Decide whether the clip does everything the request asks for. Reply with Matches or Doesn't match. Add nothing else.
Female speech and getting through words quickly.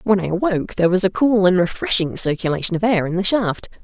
Matches